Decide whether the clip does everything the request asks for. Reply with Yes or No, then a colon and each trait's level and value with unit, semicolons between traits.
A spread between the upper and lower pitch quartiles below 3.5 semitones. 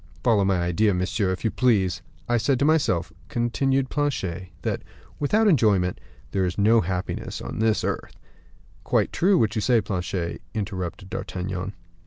No: average, 4.7 semitones